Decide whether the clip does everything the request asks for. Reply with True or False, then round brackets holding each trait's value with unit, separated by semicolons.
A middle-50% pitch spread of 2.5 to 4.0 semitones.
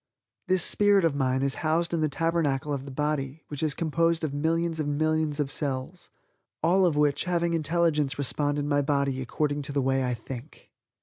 True (2.9 semitones)